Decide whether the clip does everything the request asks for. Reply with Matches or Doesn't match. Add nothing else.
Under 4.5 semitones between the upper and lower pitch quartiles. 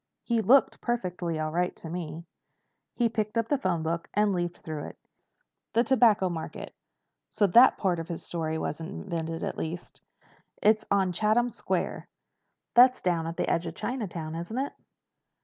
Doesn't match